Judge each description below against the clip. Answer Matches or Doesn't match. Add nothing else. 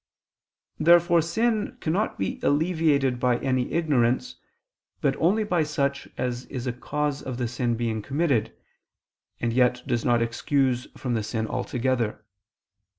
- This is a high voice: Doesn't match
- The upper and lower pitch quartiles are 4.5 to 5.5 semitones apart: Matches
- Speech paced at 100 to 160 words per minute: Matches